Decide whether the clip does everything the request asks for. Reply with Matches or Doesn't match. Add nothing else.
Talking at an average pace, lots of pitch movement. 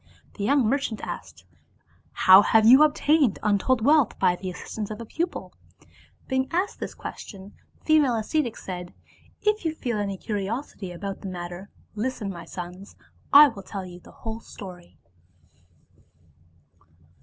Matches